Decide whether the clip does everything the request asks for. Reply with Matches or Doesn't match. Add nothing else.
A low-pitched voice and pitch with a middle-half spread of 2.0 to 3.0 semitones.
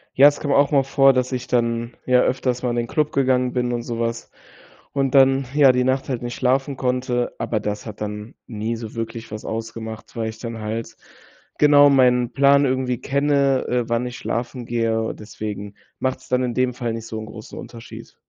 Matches